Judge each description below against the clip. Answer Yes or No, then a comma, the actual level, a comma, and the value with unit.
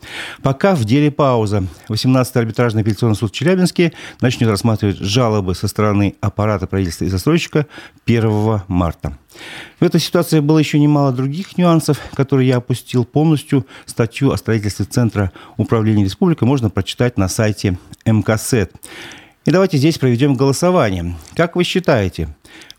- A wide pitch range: Yes, wide, 5.8 semitones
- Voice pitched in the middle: No, low, 120 Hz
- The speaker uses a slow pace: No, average, 135 wpm